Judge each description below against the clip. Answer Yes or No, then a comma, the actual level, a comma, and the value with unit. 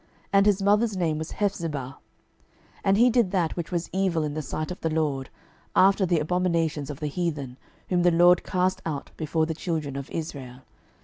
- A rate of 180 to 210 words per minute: Yes, average, 195 wpm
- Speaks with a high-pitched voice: No, medium, 165 Hz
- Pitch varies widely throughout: No, average, 3.4 semitones